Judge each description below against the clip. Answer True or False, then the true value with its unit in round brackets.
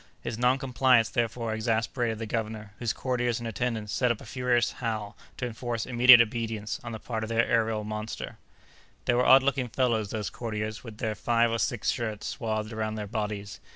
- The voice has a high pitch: False (115 Hz)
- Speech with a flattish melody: True (1.9 semitones)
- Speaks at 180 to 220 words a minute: True (190 wpm)